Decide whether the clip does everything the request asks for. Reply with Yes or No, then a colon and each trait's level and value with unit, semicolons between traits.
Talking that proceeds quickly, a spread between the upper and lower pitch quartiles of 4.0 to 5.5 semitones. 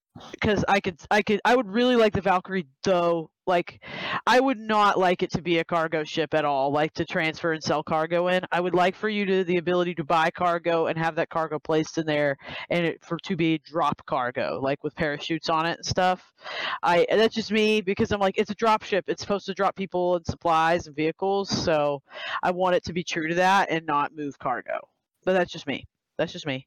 No: fast, 235 wpm; average, 3.3 semitones